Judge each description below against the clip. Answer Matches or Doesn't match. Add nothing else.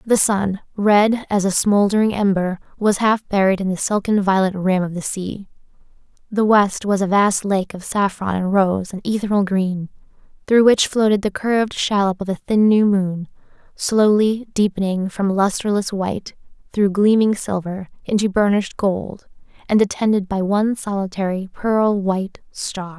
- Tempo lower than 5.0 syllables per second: Matches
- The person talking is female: Matches